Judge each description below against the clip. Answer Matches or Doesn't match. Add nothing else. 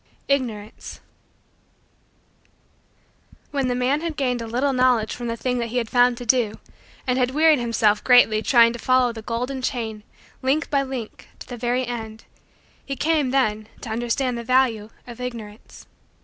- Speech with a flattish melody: Matches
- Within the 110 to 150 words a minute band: Doesn't match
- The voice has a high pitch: Matches